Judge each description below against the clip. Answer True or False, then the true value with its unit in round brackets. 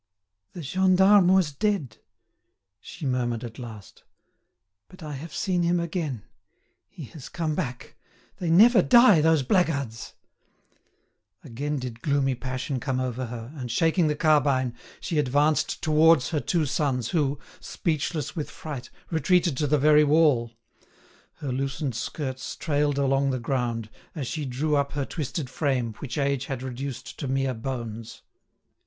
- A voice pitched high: False (140 Hz)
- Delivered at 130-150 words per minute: True (145 wpm)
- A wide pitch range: False (3.8 semitones)